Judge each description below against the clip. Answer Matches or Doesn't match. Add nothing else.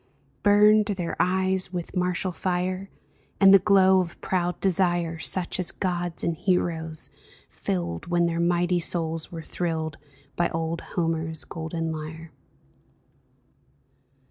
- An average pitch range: Doesn't match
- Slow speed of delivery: Matches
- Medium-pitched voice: Matches